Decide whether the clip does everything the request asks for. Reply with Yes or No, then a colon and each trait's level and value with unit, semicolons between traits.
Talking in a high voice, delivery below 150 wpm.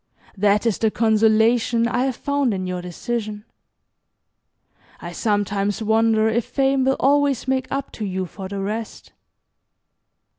Yes: high, 220 Hz; average, 140 wpm